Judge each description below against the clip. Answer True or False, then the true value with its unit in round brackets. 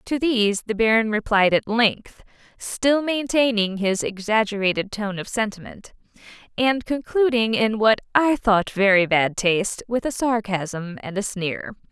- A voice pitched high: True (220 Hz)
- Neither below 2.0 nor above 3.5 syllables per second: True (3.2 syllables/s)